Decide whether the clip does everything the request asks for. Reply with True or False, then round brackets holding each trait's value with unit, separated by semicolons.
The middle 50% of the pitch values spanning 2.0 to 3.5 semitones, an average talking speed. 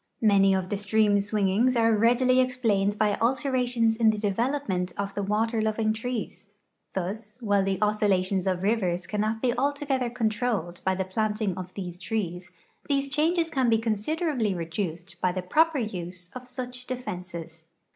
False (4.5 semitones; 160 wpm)